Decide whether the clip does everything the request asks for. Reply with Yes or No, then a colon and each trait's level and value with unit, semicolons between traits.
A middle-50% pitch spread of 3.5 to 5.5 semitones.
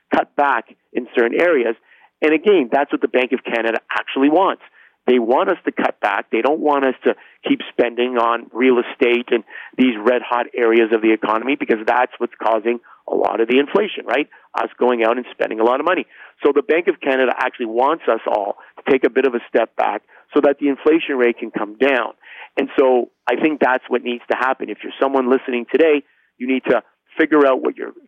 No: average, 3.0 semitones